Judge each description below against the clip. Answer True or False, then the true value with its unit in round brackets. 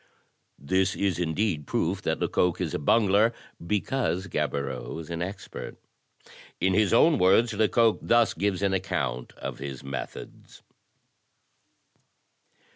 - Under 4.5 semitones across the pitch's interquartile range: False (4.8 semitones)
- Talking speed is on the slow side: True (120 wpm)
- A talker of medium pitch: False (95 Hz)